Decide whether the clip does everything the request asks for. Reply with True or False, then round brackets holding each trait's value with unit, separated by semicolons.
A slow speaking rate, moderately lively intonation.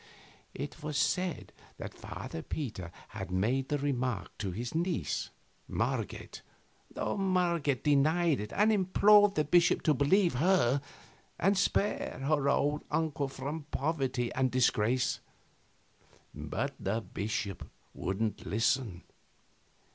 False (115 wpm; 6.0 semitones)